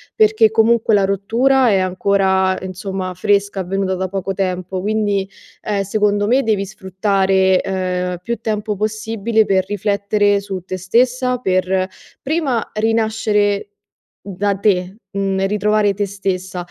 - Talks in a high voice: Yes, high, 200 Hz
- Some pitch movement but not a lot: No, narrow, 2.2 semitones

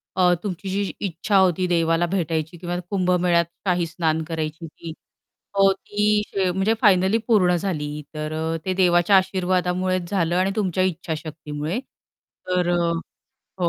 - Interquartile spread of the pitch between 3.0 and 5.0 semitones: No, narrow, 2.5 semitones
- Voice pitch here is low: No, medium, 180 Hz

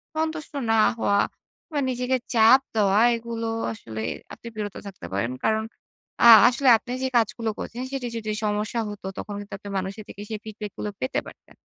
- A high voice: Yes, high, 220 Hz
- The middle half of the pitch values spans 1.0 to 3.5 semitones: Yes, average, 3.0 semitones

